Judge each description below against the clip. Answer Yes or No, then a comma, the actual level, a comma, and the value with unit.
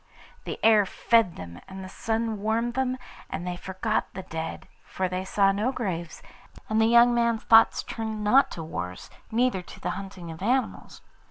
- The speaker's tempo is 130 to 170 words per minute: No, average, 180 wpm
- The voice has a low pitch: No, high, 210 Hz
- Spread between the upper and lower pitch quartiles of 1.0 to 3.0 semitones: No, average, 4.0 semitones